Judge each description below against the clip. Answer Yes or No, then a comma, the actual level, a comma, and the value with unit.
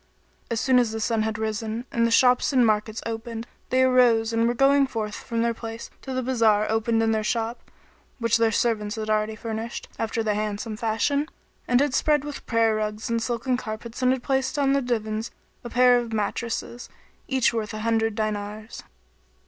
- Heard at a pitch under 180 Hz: No, high, 230 Hz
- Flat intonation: Yes, narrow, 2.2 semitones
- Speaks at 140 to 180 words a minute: No, average, 190 wpm